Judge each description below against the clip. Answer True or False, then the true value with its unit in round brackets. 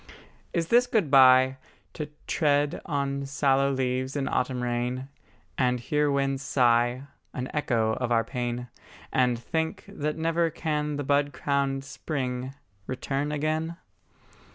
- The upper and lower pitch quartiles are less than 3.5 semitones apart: True (2.7 semitones)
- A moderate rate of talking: False (130 wpm)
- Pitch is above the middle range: False (135 Hz)